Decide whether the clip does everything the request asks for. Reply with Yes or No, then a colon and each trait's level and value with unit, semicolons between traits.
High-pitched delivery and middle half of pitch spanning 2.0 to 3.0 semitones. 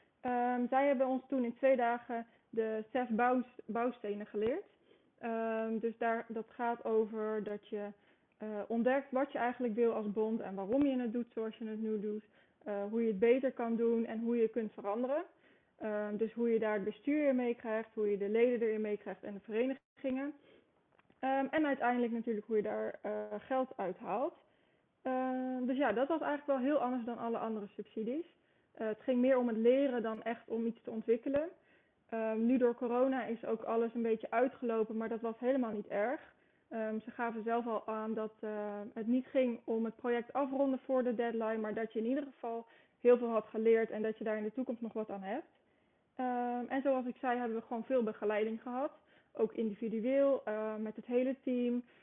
Yes: high, 230 Hz; narrow, 2.5 semitones